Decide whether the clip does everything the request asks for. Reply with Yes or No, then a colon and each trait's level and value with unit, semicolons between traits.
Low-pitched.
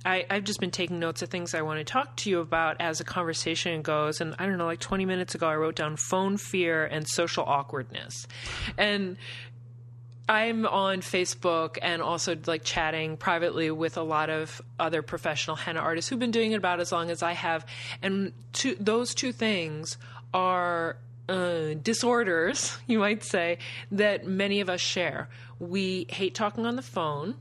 No: medium, 170 Hz